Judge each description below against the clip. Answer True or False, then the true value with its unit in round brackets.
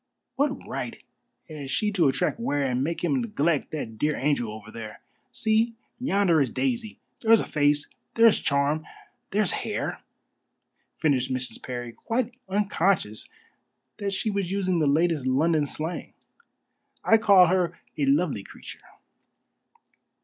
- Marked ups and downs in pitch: True (6.6 semitones)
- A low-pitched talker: False (165 Hz)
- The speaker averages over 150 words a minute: False (135 wpm)